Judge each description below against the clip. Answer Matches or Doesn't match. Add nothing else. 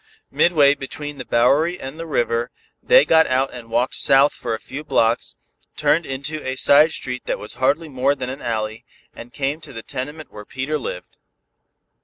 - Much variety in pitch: Doesn't match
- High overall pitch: Doesn't match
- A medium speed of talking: Matches